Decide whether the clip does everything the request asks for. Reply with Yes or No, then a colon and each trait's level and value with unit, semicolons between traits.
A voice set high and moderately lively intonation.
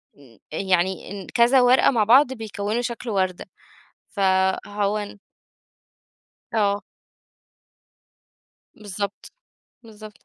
Yes: high, 205 Hz; average, 3.1 semitones